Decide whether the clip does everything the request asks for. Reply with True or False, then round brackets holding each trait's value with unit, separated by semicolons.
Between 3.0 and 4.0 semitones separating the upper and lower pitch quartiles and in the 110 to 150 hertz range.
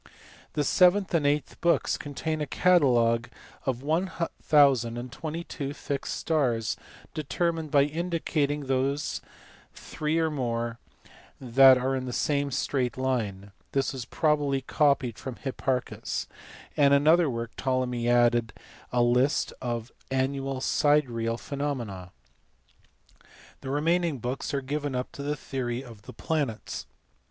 True (3.5 semitones; 135 Hz)